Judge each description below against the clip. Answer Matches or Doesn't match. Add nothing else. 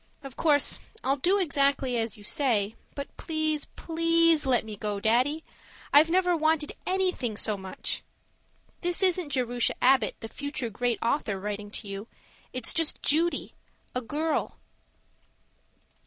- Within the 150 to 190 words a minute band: Doesn't match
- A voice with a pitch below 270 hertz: Doesn't match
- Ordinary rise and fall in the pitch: Doesn't match